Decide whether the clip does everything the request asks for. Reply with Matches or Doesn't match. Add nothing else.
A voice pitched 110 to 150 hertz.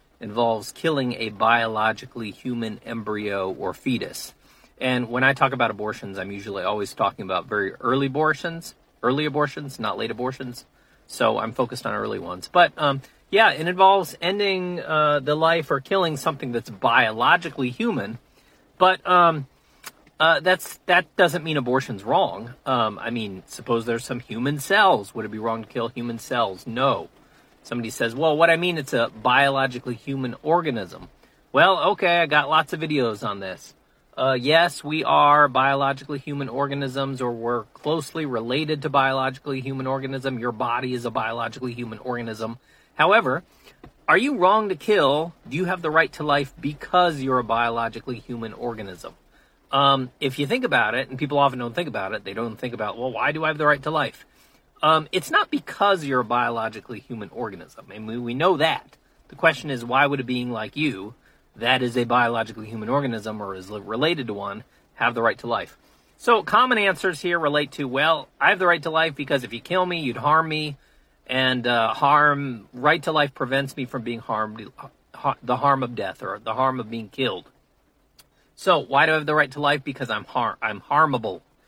Matches